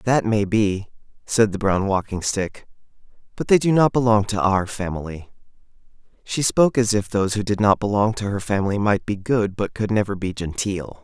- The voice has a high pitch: No, low, 105 Hz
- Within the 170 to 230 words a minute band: Yes, average, 195 wpm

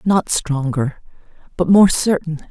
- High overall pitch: No, medium, 165 Hz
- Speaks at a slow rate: Yes, slow, 120 wpm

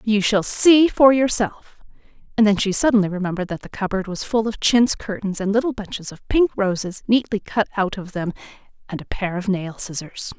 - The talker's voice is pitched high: Yes, high, 205 Hz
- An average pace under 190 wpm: No, average, 195 wpm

